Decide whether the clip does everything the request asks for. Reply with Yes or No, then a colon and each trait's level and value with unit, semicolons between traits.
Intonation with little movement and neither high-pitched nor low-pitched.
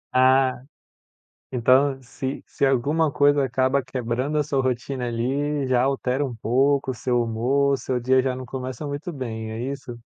No: narrow, 2.0 semitones; low, 130 Hz